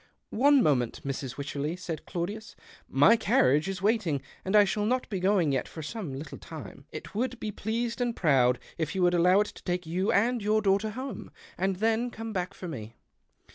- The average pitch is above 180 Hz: Yes, high, 190 Hz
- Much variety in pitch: Yes, wide, 5.9 semitones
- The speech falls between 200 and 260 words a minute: Yes, fast, 205 wpm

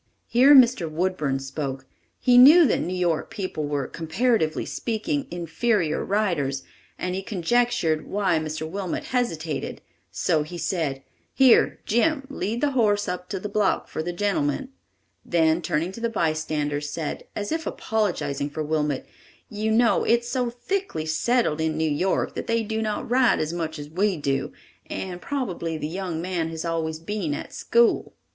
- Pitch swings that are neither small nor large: No, wide, 6.4 semitones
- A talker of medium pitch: Yes, medium, 180 Hz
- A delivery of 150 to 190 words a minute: Yes, average, 165 wpm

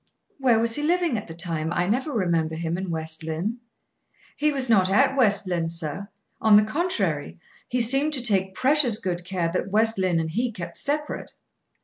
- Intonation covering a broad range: Yes, wide, 6.7 semitones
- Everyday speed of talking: Yes, average, 195 wpm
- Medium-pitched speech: No, high, 200 Hz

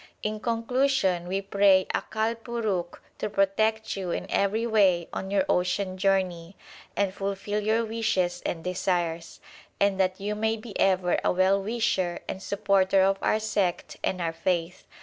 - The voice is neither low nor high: No, high, 195 Hz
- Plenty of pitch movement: No, average, 2.7 semitones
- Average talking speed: Yes, average, 155 wpm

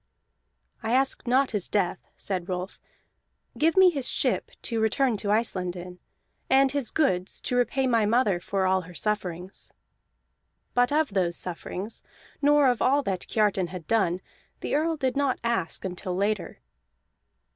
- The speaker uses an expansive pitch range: Yes, wide, 6.2 semitones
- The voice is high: Yes, high, 215 Hz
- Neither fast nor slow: Yes, average, 155 wpm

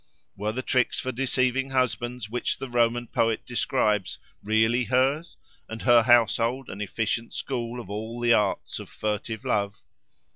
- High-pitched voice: No, low, 120 Hz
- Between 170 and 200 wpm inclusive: No, average, 150 wpm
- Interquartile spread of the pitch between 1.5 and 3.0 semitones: Yes, narrow, 2.4 semitones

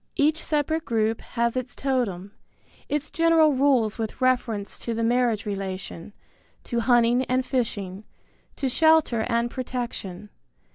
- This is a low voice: No, high, 240 Hz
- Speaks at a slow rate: Yes, slow, 130 wpm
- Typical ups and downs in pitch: Yes, average, 3.5 semitones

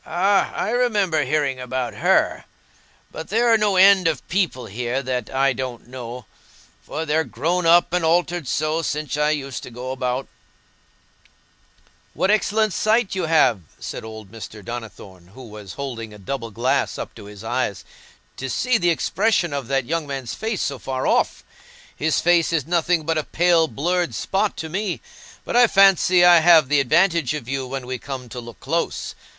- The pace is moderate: Yes, average, 180 wpm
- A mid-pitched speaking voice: Yes, medium, 150 Hz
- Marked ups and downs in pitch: Yes, wide, 5.7 semitones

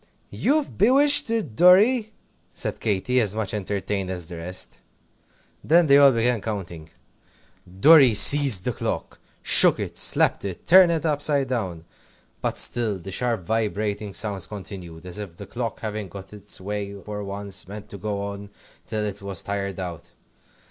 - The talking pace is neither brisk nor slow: Yes, average, 160 wpm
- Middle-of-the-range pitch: No, low, 105 Hz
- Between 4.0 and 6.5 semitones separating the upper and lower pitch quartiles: Yes, average, 4.7 semitones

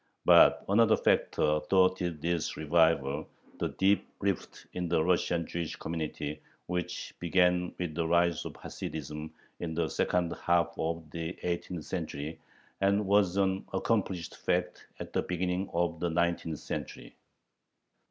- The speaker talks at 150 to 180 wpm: No, slow, 135 wpm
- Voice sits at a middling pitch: No, very low, 85 Hz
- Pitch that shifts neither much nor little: No, narrow, 2.0 semitones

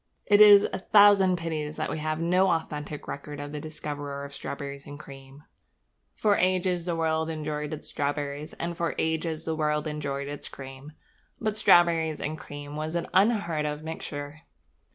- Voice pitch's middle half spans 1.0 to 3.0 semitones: Yes, average, 2.7 semitones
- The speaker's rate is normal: Yes, average, 170 wpm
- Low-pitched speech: No, medium, 155 Hz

